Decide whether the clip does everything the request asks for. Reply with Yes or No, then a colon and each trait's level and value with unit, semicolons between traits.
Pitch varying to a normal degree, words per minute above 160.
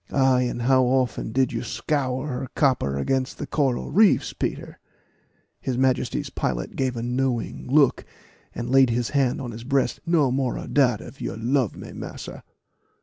No: narrow, 1.8 semitones; average, 170 wpm